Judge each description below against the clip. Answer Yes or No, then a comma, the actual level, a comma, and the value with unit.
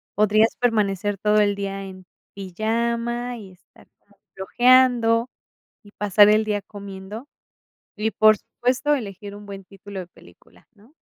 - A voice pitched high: Yes, high, 210 Hz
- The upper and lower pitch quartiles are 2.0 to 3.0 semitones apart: Yes, average, 2.7 semitones